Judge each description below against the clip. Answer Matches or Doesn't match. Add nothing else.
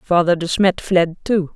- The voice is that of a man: Doesn't match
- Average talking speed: Matches